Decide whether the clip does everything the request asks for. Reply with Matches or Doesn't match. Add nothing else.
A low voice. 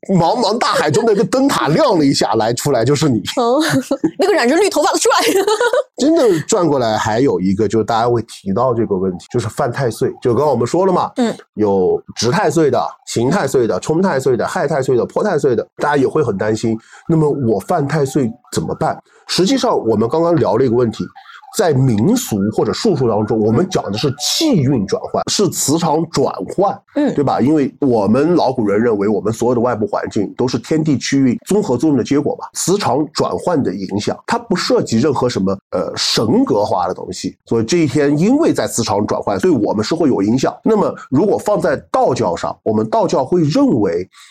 Doesn't match